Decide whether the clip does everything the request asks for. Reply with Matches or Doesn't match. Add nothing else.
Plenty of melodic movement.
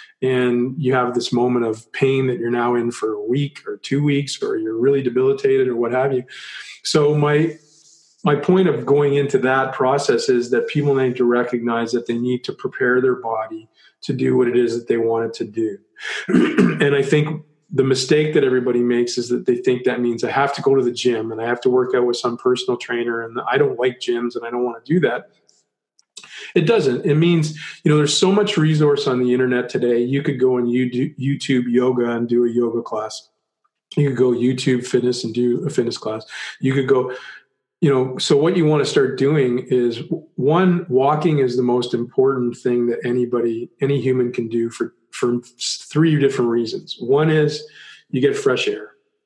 Doesn't match